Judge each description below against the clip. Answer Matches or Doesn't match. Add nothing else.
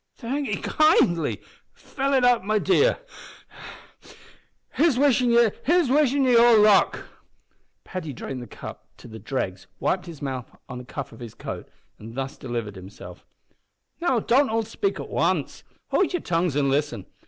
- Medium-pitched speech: Doesn't match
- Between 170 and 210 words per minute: Doesn't match